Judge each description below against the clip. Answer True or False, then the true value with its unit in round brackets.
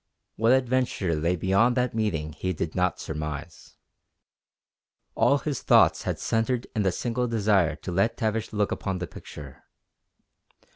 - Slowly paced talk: False (145 wpm)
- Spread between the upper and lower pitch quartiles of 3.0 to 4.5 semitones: False (5.5 semitones)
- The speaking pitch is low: True (100 Hz)